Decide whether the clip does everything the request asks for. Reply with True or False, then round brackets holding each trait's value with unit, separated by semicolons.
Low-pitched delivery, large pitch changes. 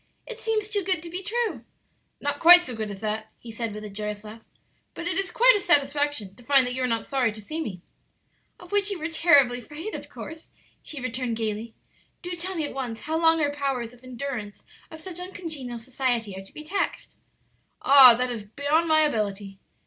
False (275 Hz; 6.6 semitones)